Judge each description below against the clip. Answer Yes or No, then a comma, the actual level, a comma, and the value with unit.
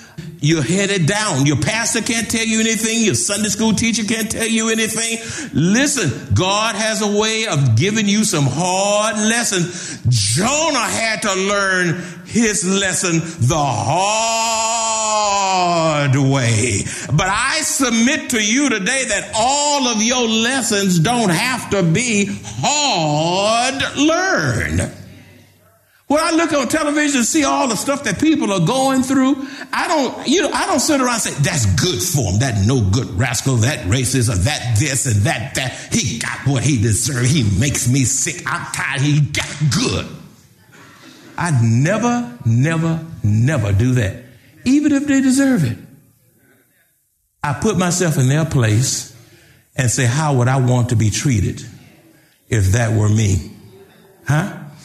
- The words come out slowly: No, average, 155 wpm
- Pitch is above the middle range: No, medium, 170 Hz